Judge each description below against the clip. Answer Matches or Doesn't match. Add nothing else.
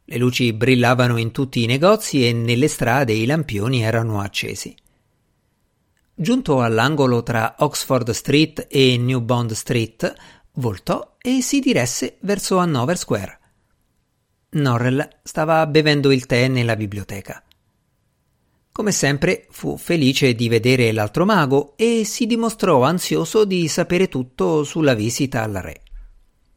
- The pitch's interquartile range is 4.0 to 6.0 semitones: Matches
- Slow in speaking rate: Doesn't match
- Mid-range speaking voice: Doesn't match